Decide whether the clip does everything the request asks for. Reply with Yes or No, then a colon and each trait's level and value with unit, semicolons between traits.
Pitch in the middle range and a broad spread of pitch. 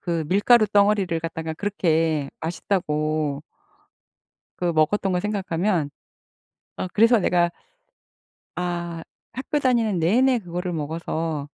No: medium, 175 Hz; average, 4.2 semitones